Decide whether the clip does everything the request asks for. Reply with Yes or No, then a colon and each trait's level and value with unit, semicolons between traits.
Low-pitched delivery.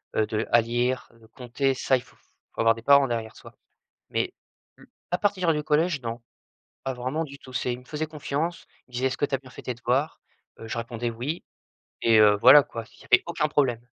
Yes: low, 130 Hz